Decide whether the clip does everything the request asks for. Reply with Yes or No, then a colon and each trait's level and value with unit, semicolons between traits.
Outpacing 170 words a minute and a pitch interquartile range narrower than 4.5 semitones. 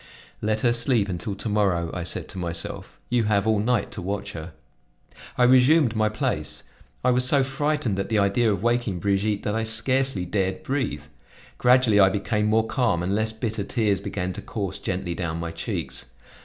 Yes: average, 190 wpm; average, 3.7 semitones